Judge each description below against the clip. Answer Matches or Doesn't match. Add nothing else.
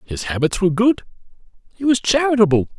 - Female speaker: Doesn't match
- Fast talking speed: Doesn't match